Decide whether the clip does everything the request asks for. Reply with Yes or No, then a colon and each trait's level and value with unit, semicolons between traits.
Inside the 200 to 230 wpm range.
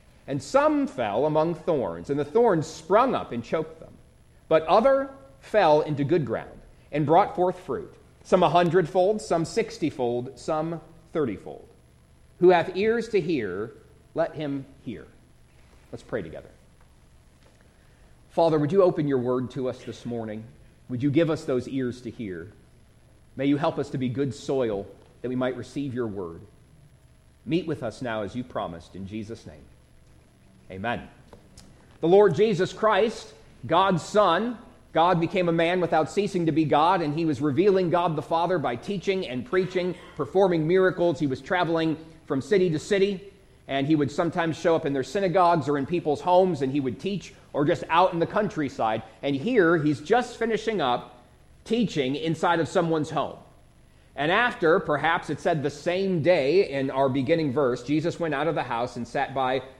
No: average, 175 wpm